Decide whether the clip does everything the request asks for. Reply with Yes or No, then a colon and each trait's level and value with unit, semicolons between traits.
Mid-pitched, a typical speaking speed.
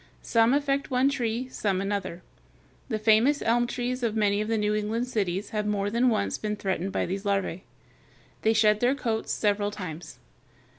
No: high, 215 Hz; average, 180 wpm